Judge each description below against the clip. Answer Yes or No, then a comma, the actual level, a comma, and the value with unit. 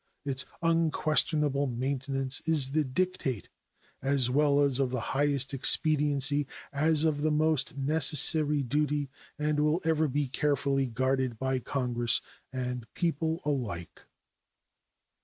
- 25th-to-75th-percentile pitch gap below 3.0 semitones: Yes, narrow, 2.5 semitones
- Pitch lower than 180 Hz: Yes, medium, 140 Hz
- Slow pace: Yes, slow, 115 wpm